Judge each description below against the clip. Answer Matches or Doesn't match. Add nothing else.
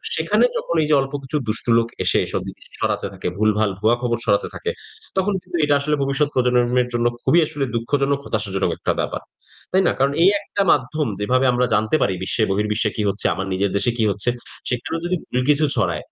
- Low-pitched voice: Matches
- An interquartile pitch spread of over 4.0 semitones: Matches